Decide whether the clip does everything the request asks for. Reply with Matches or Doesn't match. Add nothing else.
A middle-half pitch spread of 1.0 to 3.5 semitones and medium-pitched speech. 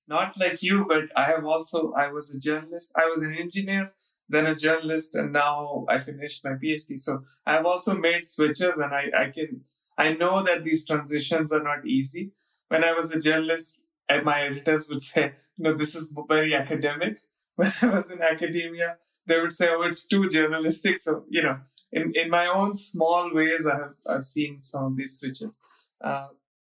Matches